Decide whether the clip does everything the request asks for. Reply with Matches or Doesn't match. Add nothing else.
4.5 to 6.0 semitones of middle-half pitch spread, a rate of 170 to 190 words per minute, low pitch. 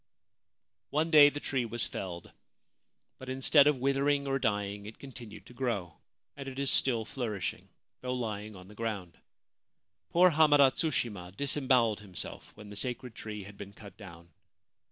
Doesn't match